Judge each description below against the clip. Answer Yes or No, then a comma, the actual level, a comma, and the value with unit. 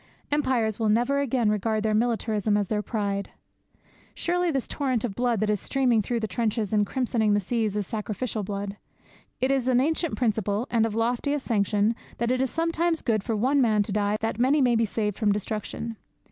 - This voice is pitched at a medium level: No, high, 225 Hz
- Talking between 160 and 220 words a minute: Yes, average, 200 wpm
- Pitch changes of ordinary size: Yes, average, 3.2 semitones